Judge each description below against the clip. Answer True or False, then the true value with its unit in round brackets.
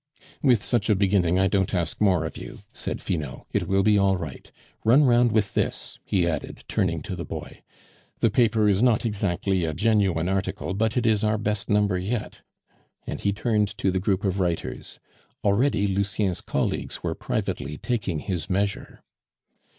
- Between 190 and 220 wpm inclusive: False (175 wpm)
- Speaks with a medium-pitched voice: False (100 Hz)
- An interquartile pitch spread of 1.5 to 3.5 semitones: True (2.5 semitones)